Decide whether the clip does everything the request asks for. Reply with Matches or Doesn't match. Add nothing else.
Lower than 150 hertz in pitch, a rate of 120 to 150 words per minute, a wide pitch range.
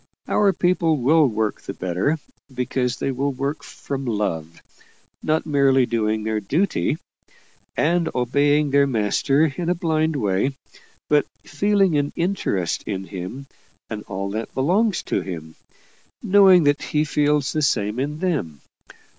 Matches